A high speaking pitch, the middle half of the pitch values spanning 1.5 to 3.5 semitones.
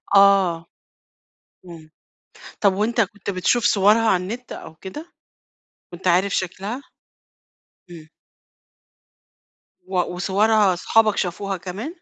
Yes: high, 195 Hz; average, 3.1 semitones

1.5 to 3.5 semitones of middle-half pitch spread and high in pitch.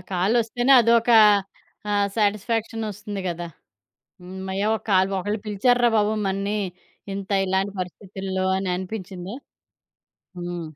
Yes: narrow, 2.5 semitones; high, 200 Hz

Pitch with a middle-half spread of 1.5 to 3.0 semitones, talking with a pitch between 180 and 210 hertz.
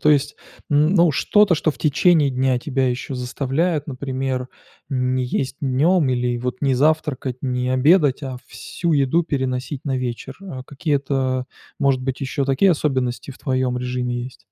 No: average, 2.7 semitones; low, 135 Hz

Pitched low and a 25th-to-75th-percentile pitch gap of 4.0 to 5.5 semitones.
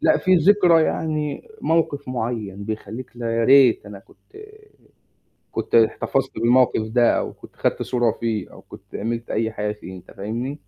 Yes: low, 120 Hz; average, 4.5 semitones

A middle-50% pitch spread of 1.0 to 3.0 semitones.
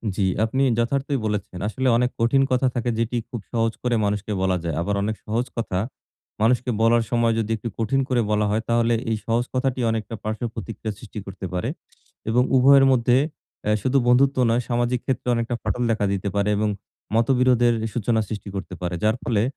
Yes: narrow, 2.5 semitones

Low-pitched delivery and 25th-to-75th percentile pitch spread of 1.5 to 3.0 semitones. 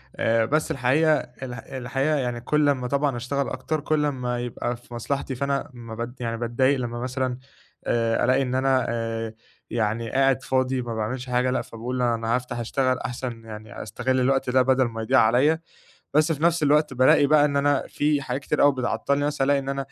Yes: low, 130 Hz; average, 2.7 semitones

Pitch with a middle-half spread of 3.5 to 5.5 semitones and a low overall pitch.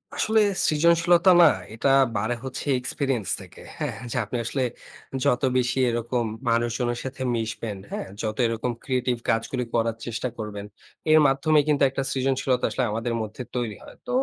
No: average, 2.8 semitones; low, 125 Hz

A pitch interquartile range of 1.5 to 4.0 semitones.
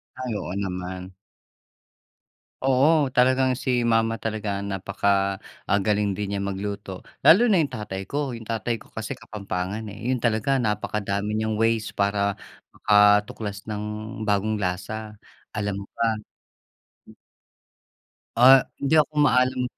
Yes: average, 3.5 semitones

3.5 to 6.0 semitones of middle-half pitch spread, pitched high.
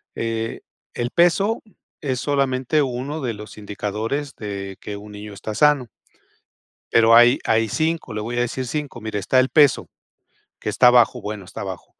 No: average, 4.5 semitones; low, 120 Hz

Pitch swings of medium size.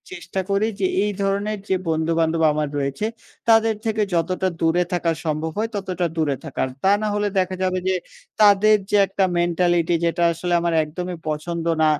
Yes: average, 3.4 semitones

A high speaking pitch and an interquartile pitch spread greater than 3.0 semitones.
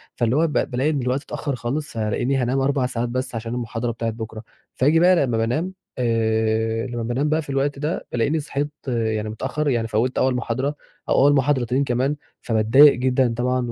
No: low, 125 Hz; average, 3.4 semitones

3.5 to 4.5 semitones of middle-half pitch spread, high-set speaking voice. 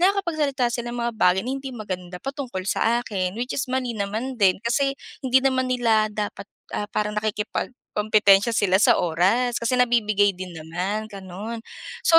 Yes: average, 4.1 semitones; high, 215 Hz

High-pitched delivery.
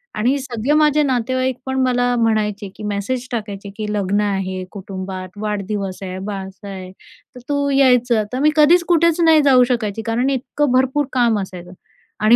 Yes: high, 230 Hz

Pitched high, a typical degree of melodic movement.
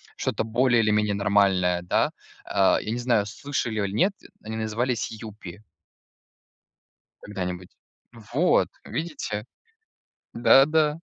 No: low, 110 Hz; average, 3.5 semitones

